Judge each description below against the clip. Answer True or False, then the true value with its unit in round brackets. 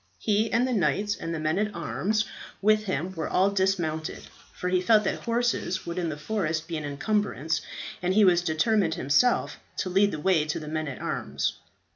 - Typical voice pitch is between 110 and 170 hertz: False (185 Hz)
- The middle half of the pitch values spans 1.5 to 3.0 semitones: False (4.8 semitones)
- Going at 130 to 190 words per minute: False (200 wpm)